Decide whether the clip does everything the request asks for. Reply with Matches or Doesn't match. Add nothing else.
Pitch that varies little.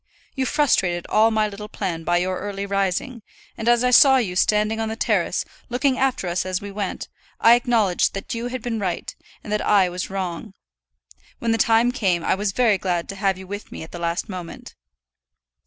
Doesn't match